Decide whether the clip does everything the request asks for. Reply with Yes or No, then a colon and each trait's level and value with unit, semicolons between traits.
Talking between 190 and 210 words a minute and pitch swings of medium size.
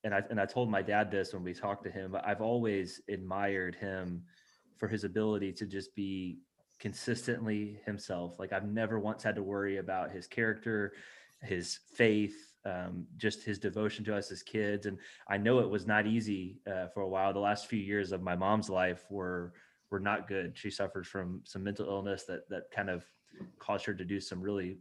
No: fast, 205 wpm; narrow, 1.9 semitones